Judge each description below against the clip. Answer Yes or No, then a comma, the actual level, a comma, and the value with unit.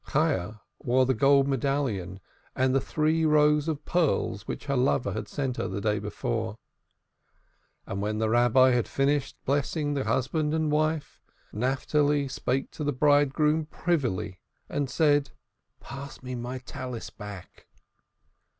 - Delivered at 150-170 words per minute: No, slow, 135 wpm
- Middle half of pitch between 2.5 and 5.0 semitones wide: Yes, average, 3.6 semitones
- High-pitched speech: No, low, 135 Hz